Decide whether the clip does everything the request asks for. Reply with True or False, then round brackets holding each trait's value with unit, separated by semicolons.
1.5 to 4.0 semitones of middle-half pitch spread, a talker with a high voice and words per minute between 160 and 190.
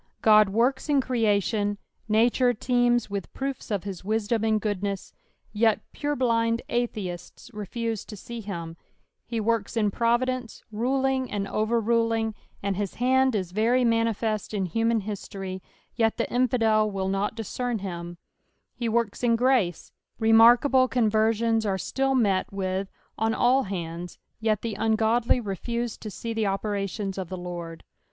False (3.0 semitones; 220 Hz; 150 wpm)